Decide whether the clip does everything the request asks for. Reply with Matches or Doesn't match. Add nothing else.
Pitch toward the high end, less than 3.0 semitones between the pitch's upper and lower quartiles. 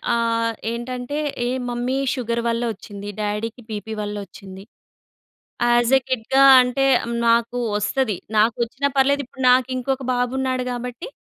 Matches